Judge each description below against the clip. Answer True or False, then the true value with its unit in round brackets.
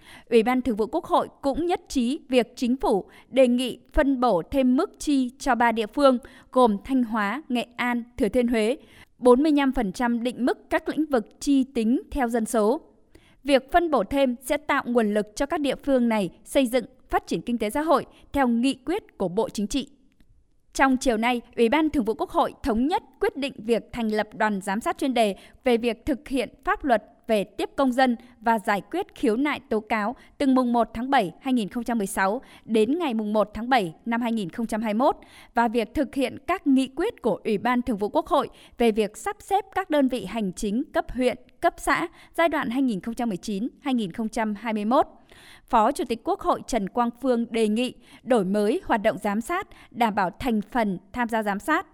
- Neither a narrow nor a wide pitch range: True (3.8 semitones)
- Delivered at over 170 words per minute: True (205 wpm)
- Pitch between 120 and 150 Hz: False (250 Hz)